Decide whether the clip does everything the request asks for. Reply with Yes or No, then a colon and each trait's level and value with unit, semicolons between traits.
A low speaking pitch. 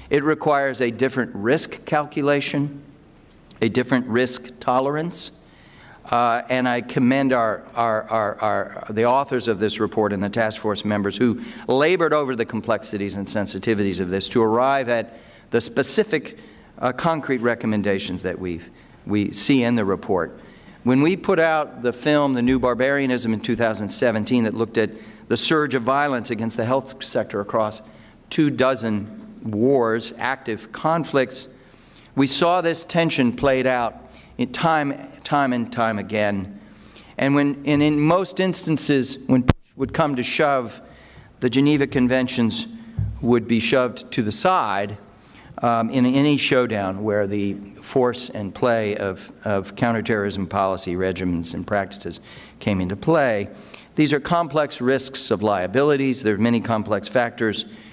Yes: low, 120 Hz